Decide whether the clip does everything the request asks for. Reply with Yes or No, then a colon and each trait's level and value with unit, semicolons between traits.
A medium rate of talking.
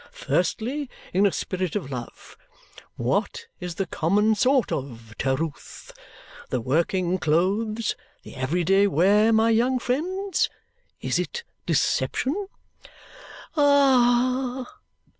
No: slow, 110 wpm